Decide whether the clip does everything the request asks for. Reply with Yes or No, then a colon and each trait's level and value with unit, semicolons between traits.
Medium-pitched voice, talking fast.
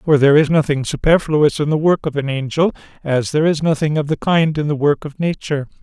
Yes: medium, 150 Hz; fast, 235 wpm